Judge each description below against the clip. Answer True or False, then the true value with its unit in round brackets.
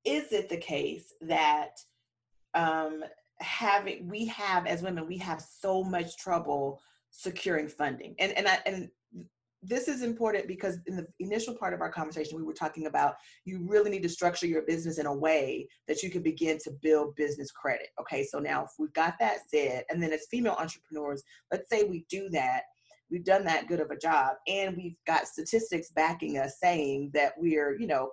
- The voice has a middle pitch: True (170 Hz)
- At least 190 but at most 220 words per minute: True (195 wpm)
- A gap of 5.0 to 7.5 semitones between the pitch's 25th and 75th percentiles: False (3.8 semitones)